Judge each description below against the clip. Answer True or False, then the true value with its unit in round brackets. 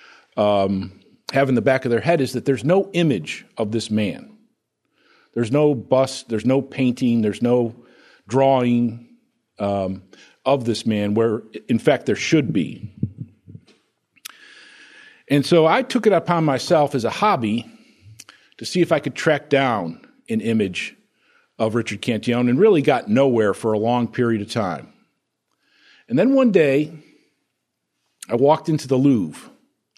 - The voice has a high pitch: False (130 Hz)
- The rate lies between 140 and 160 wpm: True (150 wpm)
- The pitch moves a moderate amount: False (6.4 semitones)